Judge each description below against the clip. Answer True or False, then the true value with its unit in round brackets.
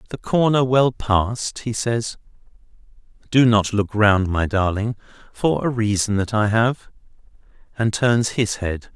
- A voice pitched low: True (110 Hz)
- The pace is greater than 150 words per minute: False (145 wpm)